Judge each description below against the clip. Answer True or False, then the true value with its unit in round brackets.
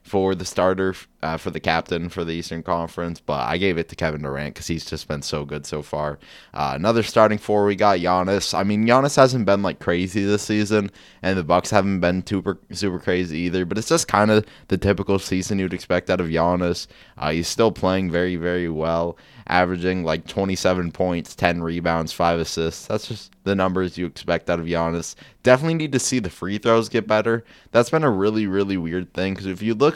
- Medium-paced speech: False (220 wpm)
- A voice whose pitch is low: True (95 Hz)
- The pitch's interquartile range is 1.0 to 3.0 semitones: False (3.4 semitones)